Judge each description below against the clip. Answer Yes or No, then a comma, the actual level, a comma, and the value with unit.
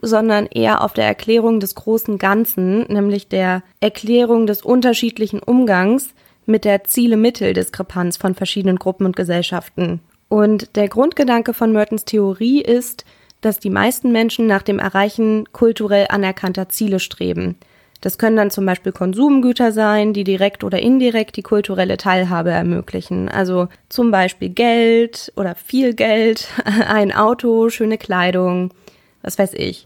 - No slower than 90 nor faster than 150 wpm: Yes, average, 140 wpm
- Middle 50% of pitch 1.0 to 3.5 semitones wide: Yes, average, 3.2 semitones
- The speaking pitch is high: Yes, high, 210 Hz